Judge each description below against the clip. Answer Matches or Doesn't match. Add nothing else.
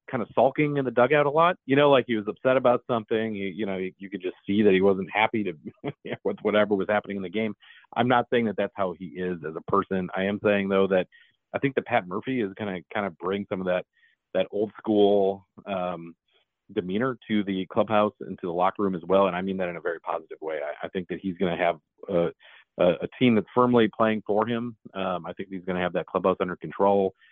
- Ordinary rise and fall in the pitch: Matches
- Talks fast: Matches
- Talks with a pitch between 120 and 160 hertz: Doesn't match